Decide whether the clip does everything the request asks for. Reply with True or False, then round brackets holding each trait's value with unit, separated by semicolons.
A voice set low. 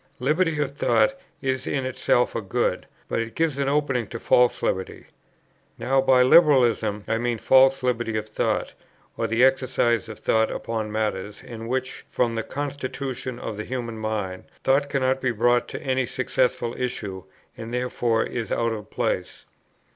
True (125 Hz)